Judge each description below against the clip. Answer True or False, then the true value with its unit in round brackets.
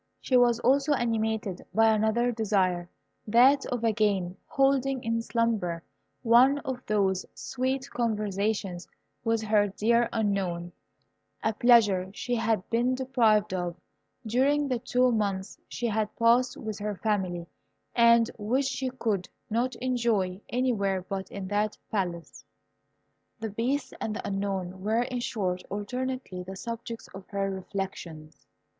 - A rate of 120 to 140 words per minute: True (135 wpm)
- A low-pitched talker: False (220 Hz)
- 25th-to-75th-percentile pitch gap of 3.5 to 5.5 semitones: True (3.8 semitones)